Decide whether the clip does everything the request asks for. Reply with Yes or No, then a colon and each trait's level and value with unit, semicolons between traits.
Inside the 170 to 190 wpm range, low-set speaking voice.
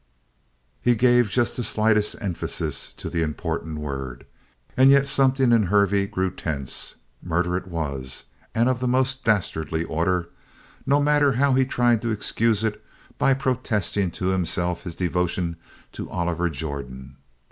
No: average, 145 wpm; low, 100 Hz